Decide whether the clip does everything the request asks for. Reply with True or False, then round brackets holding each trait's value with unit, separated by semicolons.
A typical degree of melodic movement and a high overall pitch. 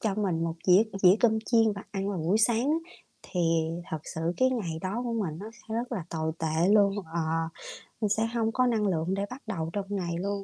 True (4.2 semitones; 200 Hz)